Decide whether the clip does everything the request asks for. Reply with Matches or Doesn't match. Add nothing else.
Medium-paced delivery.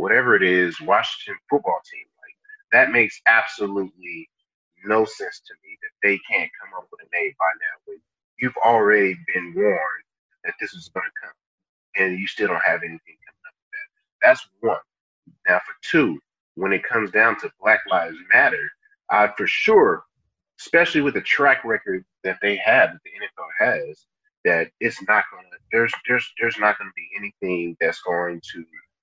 Matches